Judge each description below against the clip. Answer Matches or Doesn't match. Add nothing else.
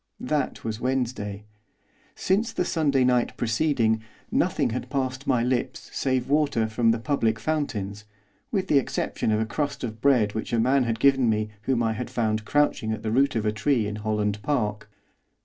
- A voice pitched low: Matches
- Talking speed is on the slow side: Doesn't match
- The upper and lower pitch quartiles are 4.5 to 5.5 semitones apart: Doesn't match